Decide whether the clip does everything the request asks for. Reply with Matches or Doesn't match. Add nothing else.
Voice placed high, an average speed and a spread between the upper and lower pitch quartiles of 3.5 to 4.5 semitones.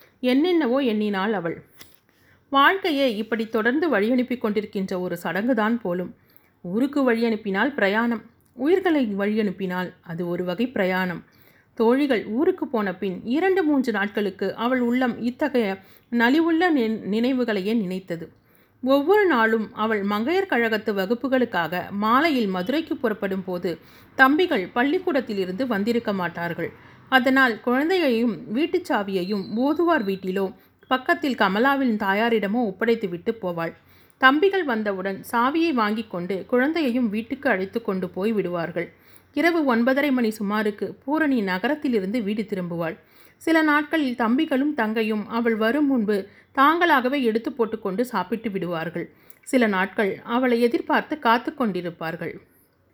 Doesn't match